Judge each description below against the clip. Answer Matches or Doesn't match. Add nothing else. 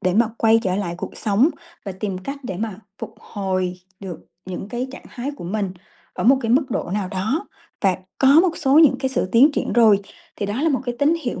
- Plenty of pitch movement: Matches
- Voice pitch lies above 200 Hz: Matches